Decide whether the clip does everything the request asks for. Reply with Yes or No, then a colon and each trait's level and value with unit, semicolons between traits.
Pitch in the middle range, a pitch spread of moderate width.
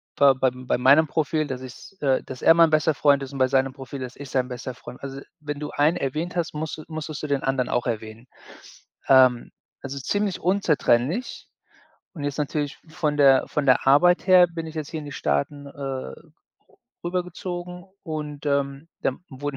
Yes: medium, 145 Hz; average, 3.1 semitones